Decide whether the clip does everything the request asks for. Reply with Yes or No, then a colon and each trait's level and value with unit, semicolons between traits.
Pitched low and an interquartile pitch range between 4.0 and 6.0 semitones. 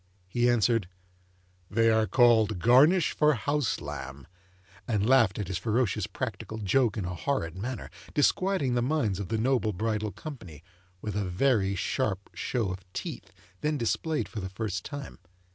Yes: low, 110 Hz; average, 5.1 semitones